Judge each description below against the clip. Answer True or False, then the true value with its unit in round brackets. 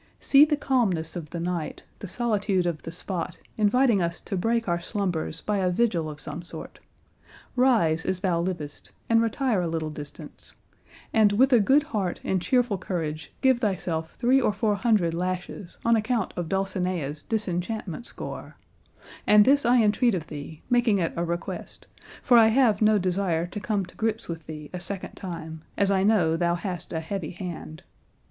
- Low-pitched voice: False (190 Hz)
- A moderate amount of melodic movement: True (4.8 semitones)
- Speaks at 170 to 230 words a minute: True (180 wpm)